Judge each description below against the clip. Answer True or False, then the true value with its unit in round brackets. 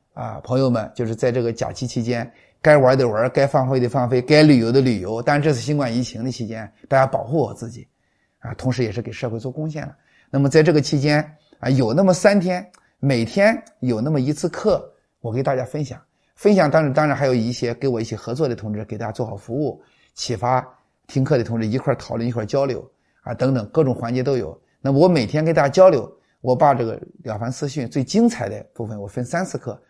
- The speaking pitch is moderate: False (130 Hz)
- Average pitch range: True (3.9 semitones)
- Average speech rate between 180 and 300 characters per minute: False (325 characters per minute)